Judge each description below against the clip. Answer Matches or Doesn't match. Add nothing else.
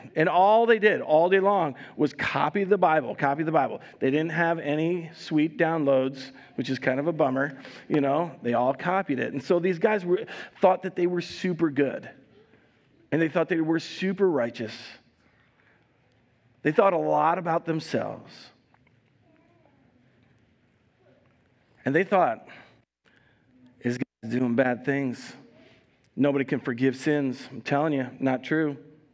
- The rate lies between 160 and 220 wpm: Doesn't match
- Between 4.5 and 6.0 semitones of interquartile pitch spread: Matches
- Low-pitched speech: Doesn't match